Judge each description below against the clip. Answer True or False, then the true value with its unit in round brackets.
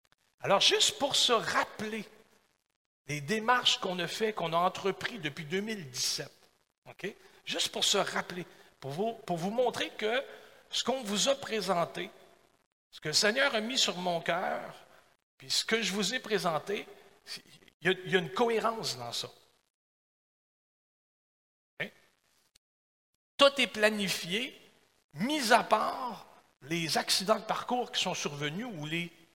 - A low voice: False (200 Hz)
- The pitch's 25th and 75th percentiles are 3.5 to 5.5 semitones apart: True (4.9 semitones)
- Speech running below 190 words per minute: True (150 wpm)